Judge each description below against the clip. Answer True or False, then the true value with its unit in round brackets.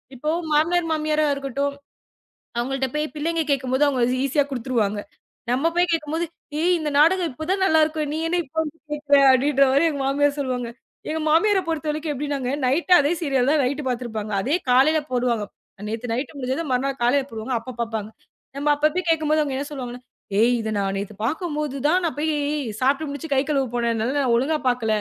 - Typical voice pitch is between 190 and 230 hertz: False (280 Hz)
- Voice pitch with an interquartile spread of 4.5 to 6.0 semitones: False (3.7 semitones)